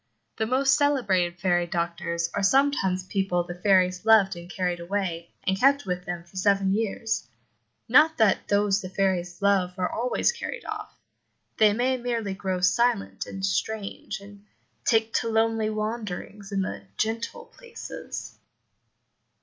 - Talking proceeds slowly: No, average, 145 wpm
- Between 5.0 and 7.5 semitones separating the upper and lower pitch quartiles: No, average, 3.6 semitones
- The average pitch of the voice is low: No, high, 200 Hz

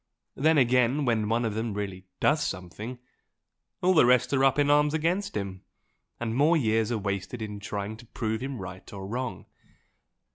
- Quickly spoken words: No, average, 180 wpm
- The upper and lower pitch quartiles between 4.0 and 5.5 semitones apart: Yes, average, 5.1 semitones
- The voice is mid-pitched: No, low, 115 Hz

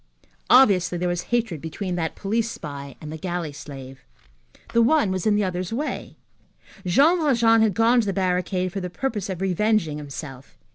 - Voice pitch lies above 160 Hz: Yes, medium, 185 Hz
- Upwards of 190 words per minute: No, average, 180 wpm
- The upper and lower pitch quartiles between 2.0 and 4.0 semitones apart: No, wide, 5.4 semitones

